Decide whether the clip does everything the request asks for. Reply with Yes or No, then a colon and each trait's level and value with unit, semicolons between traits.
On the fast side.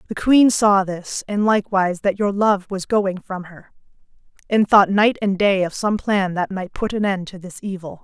Yes: fast, 215 wpm